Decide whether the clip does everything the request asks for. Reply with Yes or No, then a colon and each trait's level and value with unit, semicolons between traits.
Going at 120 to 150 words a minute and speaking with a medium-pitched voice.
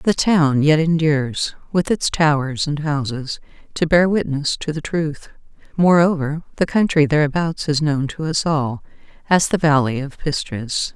No: average, 160 wpm; medium, 150 Hz